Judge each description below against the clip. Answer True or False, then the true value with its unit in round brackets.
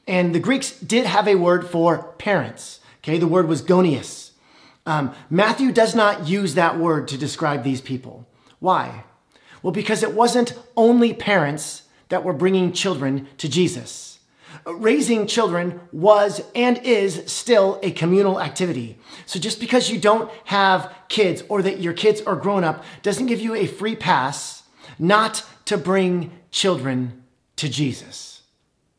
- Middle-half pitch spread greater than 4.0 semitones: True (5.2 semitones)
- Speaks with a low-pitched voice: False (185 Hz)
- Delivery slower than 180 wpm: True (150 wpm)